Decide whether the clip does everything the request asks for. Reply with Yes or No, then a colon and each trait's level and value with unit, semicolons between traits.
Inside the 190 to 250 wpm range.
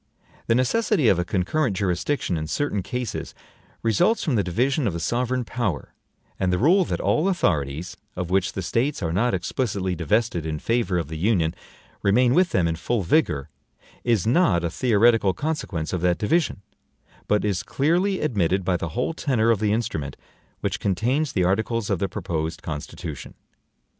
No: average, 175 wpm